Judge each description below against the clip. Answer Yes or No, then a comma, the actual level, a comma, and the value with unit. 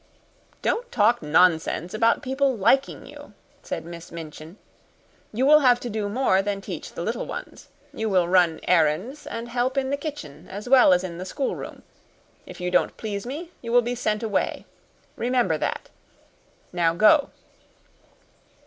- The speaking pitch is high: Yes, high, 215 Hz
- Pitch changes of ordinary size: No, wide, 6.1 semitones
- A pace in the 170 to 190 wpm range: No, average, 160 wpm